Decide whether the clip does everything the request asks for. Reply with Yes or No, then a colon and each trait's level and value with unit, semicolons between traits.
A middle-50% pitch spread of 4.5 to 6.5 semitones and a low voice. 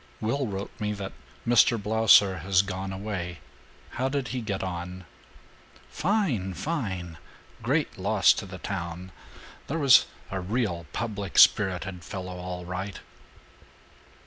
No: average, 3.6 semitones; very low, 95 Hz